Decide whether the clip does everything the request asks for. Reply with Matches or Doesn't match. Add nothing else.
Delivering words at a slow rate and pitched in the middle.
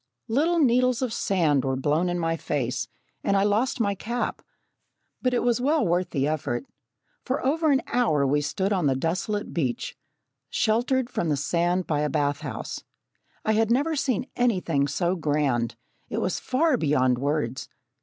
Doesn't match